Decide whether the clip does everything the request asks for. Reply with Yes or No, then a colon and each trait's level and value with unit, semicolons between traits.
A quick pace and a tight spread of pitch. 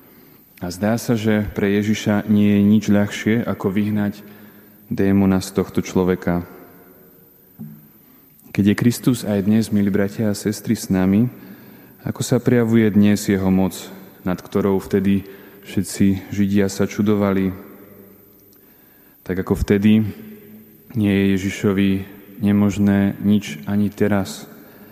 No: average, 120 wpm; narrow, 1.3 semitones